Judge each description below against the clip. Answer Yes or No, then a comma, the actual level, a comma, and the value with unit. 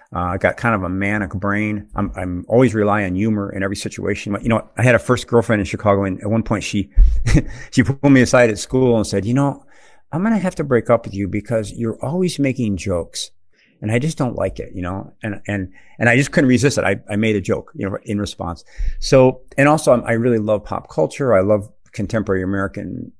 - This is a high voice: No, low, 110 Hz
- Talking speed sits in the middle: No, fast, 240 wpm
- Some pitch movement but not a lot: Yes, average, 3.7 semitones